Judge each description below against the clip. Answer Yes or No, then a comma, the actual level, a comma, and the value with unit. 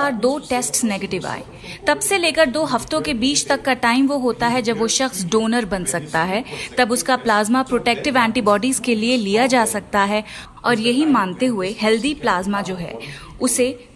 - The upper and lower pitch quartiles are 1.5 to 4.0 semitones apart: Yes, average, 3.7 semitones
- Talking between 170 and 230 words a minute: Yes, fast, 190 wpm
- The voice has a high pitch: Yes, high, 240 Hz